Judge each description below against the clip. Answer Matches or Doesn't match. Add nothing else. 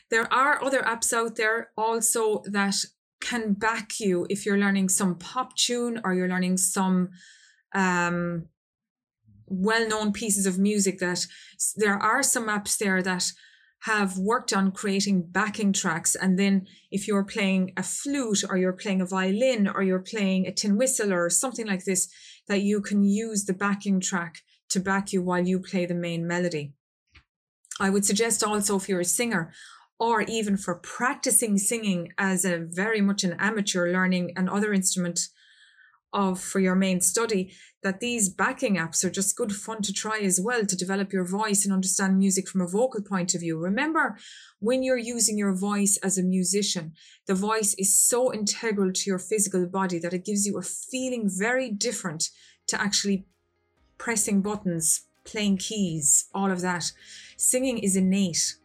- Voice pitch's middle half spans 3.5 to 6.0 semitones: Doesn't match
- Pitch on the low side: Doesn't match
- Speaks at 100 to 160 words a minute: Doesn't match